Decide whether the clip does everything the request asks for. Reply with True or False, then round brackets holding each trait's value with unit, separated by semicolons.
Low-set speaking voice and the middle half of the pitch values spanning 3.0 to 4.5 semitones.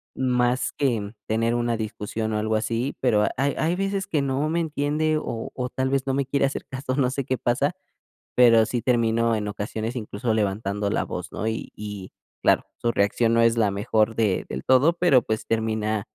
True (115 Hz; 3.5 semitones)